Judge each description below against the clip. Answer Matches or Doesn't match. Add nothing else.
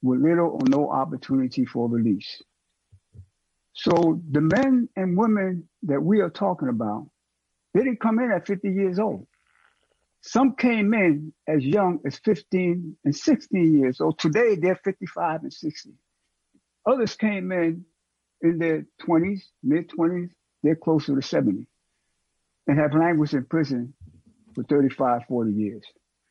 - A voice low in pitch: Doesn't match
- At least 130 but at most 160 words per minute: Matches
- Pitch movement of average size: Doesn't match